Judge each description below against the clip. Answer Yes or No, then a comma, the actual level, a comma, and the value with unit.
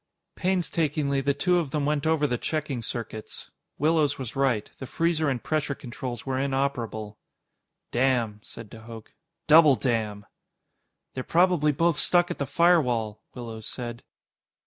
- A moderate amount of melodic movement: Yes, average, 4.6 semitones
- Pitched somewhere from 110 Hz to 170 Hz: Yes, low, 135 Hz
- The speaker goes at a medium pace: Yes, average, 145 wpm